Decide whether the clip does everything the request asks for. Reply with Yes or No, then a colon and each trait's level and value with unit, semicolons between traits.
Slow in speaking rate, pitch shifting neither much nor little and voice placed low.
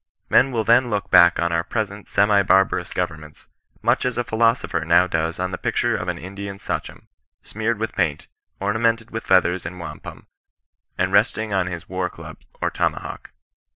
No: average, 175 wpm; average, 3.7 semitones; low, 100 Hz